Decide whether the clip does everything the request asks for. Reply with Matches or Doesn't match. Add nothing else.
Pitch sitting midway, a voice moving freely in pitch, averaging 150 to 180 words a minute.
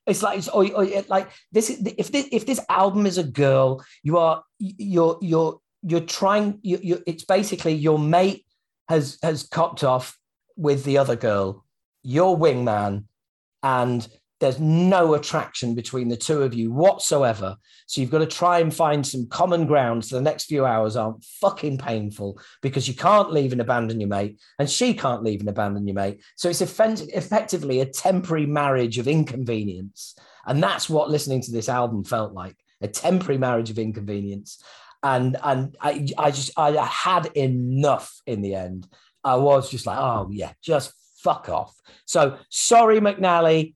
Matches